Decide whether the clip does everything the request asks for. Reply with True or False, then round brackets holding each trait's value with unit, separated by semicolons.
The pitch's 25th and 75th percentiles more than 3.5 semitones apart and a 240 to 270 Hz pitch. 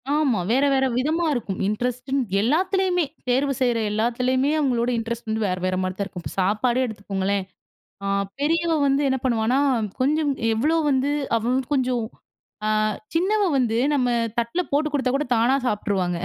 True (4.4 semitones; 250 Hz)